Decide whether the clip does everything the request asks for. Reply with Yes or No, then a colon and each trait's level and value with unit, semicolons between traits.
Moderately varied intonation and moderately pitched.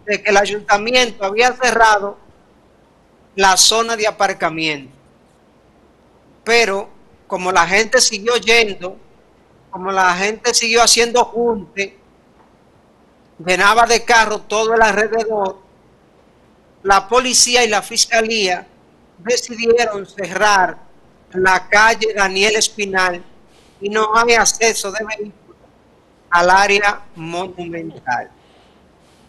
No: average, 3.1 semitones; high, 210 Hz